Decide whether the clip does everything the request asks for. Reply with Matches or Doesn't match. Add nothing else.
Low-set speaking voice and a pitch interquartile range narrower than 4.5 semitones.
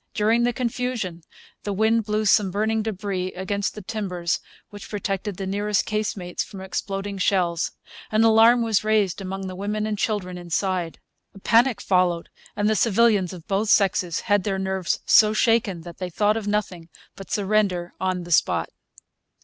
Doesn't match